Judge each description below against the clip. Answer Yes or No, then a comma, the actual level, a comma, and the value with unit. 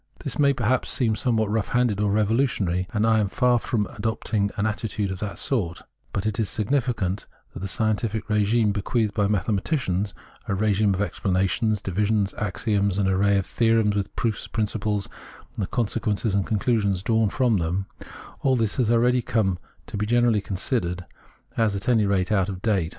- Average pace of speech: Yes, average, 185 wpm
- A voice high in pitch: No, low, 105 Hz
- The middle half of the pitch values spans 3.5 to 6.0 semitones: No, narrow, 2.4 semitones